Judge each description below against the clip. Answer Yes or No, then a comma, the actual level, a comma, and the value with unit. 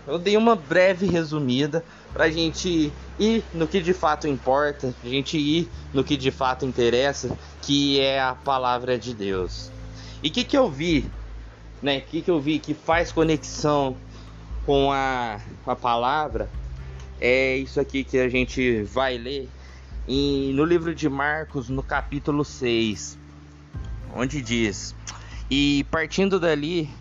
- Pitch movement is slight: No, average, 3.7 semitones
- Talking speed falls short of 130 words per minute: No, average, 150 wpm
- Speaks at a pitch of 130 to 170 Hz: Yes, low, 135 Hz